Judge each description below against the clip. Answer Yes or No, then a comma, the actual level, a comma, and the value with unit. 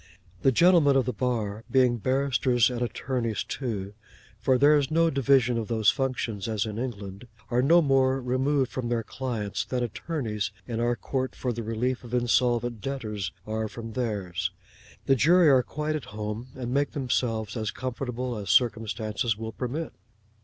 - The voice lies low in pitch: Yes, low, 120 Hz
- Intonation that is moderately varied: Yes, average, 3.1 semitones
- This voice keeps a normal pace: Yes, average, 165 wpm